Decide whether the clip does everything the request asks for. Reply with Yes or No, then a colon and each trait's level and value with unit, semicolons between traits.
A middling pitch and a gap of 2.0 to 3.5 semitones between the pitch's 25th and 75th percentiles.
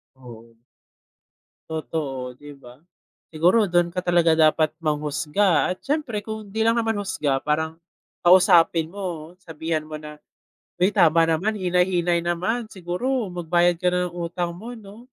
No: medium, 175 Hz; average, 3.9 semitones